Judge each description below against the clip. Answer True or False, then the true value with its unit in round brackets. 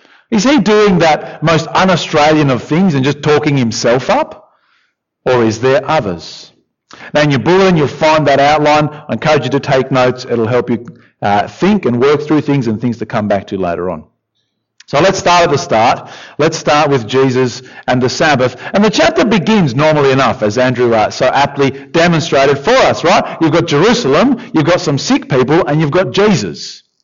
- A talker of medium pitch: True (150 Hz)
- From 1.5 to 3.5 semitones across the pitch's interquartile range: False (5.1 semitones)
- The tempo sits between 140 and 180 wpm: False (195 wpm)